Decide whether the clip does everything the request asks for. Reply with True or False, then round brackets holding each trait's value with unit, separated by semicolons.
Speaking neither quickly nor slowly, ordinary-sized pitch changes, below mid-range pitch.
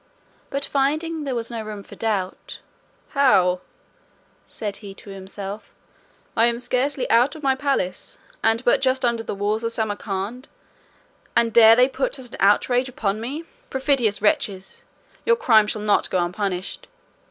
False (155 wpm; 4.4 semitones; 230 Hz)